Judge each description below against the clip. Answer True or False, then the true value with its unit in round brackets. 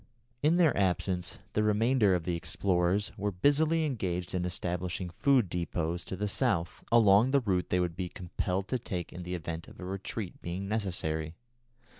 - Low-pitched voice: True (95 Hz)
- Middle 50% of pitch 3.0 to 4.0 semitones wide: True (3.4 semitones)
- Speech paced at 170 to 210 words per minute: True (175 wpm)